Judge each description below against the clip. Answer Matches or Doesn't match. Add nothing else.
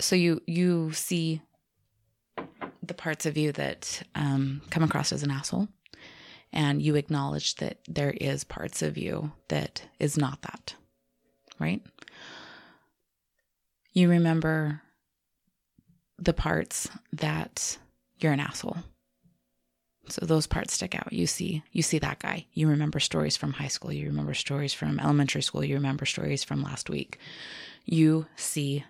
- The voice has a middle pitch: Matches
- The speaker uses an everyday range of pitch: Doesn't match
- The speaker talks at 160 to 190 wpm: Doesn't match